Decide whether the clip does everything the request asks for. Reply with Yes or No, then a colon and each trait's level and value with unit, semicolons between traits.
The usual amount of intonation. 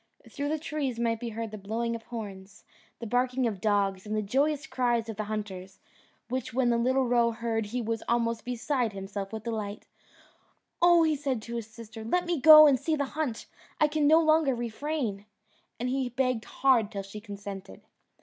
Yes: average, 3.8 semitones